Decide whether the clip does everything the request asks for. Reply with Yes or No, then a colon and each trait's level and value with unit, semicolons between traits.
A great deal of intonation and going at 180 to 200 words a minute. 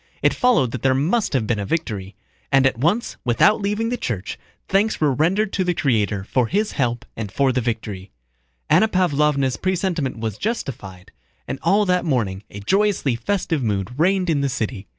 Yes: wide, 8.6 semitones; average, 185 wpm